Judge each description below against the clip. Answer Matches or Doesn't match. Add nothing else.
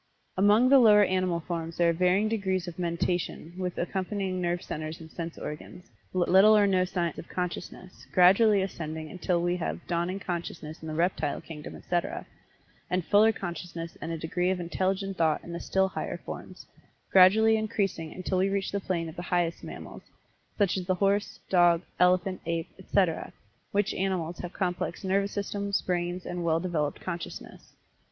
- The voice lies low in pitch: Doesn't match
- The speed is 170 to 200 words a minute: Matches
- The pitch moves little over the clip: Matches